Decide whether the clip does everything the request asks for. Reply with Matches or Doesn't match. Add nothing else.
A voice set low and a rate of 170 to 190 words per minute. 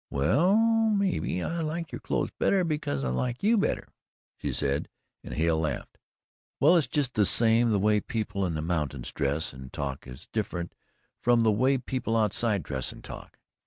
Matches